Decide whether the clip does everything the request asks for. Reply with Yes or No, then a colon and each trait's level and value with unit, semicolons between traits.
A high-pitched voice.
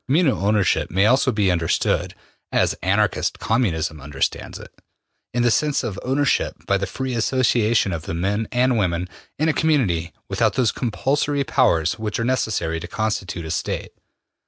No: low, 110 Hz